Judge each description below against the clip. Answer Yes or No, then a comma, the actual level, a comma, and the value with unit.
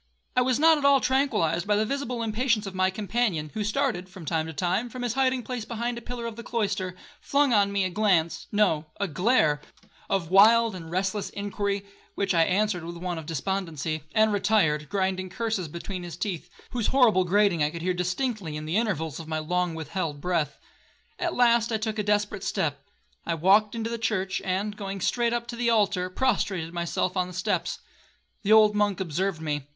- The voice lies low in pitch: No, high, 195 Hz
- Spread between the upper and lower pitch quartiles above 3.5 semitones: Yes, average, 4.7 semitones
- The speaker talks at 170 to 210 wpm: Yes, average, 200 wpm